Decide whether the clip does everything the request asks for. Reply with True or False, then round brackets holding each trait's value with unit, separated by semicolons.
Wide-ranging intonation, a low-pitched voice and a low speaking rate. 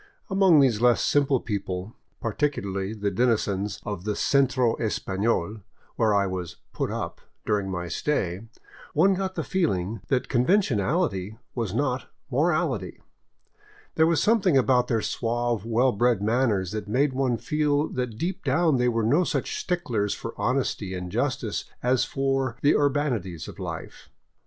False (5.7 semitones; 120 Hz; 155 wpm)